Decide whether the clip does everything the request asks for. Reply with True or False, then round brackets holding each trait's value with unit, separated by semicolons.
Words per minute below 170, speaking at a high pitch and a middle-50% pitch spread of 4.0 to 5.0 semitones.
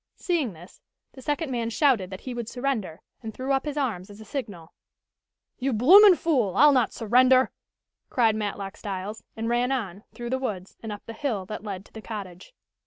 False (195 wpm; 230 Hz; 4.5 semitones)